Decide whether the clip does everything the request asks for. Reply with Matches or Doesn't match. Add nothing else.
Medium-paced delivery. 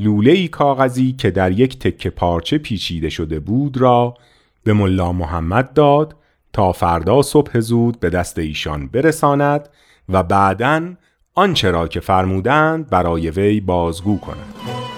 Matches